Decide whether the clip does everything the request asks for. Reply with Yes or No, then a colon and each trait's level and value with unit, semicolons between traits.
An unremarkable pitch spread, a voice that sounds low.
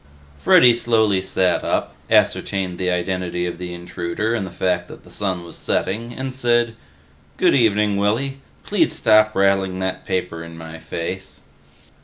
Yes: average, 3.8 semitones; very low, 95 Hz